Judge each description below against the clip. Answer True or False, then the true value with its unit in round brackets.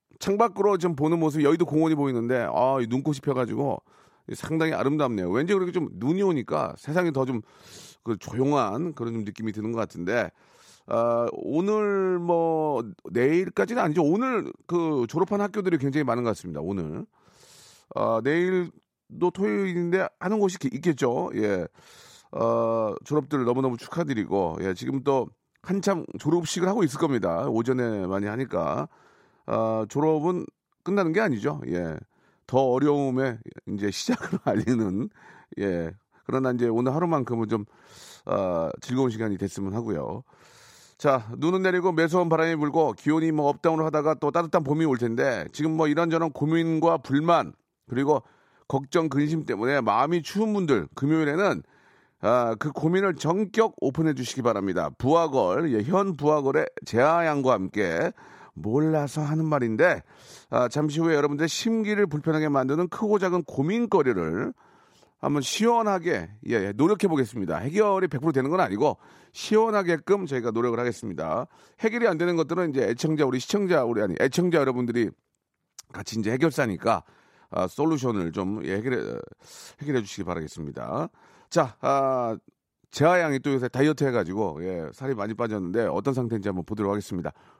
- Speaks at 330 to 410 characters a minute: True (335 characters per minute)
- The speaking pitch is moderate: True (145 Hz)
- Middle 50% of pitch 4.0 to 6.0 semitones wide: False (6.5 semitones)